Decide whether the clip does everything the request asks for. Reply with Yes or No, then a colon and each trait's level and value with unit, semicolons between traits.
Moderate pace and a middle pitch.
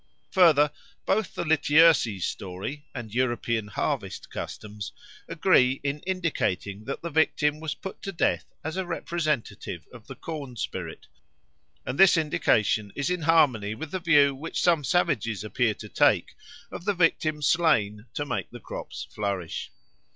Yes: average, 150 wpm; medium, 145 Hz